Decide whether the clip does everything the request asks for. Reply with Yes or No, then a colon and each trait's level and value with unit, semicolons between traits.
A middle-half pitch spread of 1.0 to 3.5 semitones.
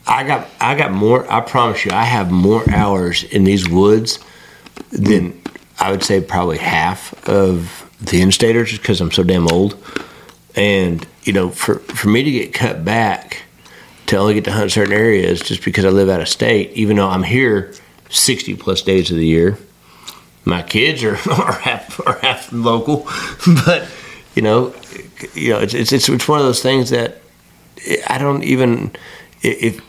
No: average, 4.2 semitones